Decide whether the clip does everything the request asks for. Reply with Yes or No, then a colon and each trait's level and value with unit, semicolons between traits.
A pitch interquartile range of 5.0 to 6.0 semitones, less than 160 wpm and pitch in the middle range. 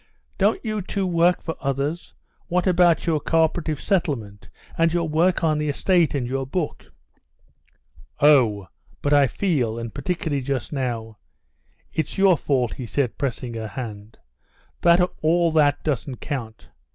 Yes: wide, 5.5 semitones; average, 140 wpm; medium, 145 Hz